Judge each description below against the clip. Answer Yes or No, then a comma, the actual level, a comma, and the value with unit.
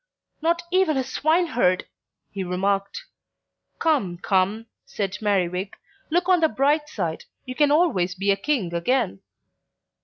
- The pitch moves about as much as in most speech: No, wide, 8.7 semitones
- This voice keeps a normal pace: No, slow, 130 wpm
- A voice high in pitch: Yes, high, 215 Hz